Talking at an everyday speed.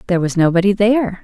Yes: average, 195 wpm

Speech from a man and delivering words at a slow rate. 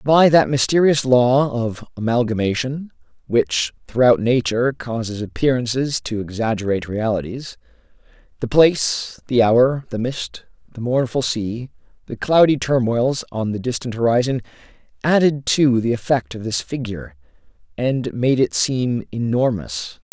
Yes: male; slow, 125 wpm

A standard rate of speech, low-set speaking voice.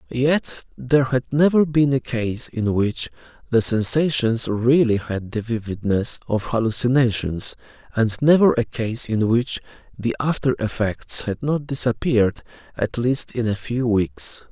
Yes: average, 145 wpm; low, 120 Hz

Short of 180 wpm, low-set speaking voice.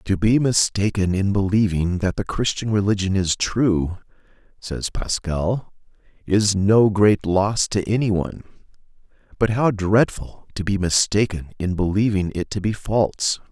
Yes: average, 140 wpm; low, 100 Hz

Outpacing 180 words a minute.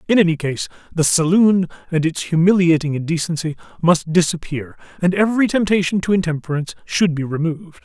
No: average, 145 wpm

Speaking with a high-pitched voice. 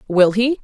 Yes: high, 215 Hz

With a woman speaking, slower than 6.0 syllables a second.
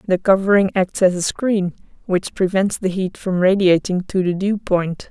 Yes: female; 4.6 syllables/s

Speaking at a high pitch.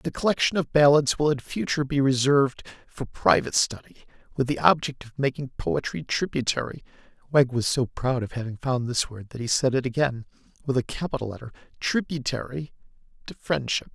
No: low, 130 Hz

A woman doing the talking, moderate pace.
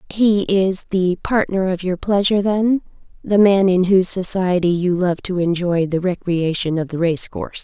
Yes: female; average, 175 wpm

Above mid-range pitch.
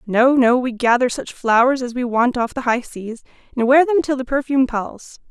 Yes: very high, 250 Hz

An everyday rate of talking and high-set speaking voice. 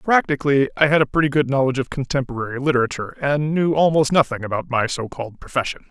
No: average, 185 wpm; medium, 140 Hz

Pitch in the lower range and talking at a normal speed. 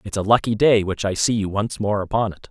No: low, 105 Hz; fast, 285 wpm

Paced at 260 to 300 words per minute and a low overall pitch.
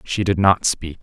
No: fast, 235 wpm; very low, 90 Hz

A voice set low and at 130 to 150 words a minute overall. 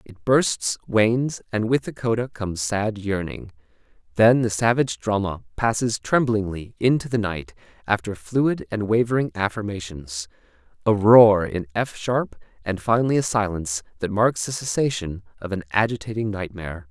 Yes: low, 105 Hz; average, 145 wpm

